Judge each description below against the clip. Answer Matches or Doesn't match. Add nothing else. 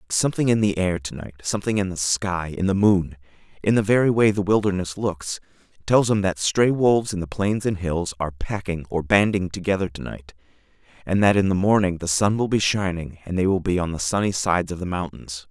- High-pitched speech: Doesn't match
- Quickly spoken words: Matches